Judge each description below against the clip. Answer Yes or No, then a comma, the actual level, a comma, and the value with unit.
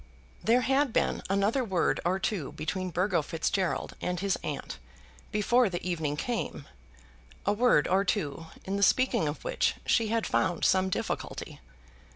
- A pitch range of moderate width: Yes, average, 4.3 semitones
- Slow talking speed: No, average, 155 wpm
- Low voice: No, high, 190 Hz